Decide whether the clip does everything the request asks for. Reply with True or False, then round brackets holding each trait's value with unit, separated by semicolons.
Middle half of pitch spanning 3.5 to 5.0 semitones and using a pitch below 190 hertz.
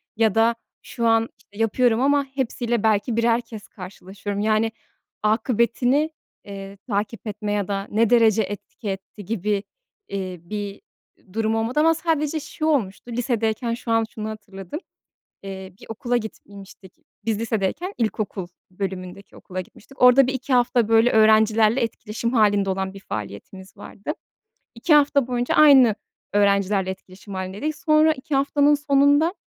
False (3.9 semitones; 220 Hz)